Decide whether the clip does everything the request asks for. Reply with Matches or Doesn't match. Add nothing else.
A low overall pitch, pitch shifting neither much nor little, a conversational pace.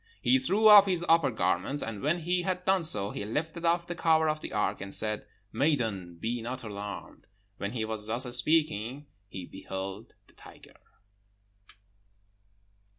Doesn't match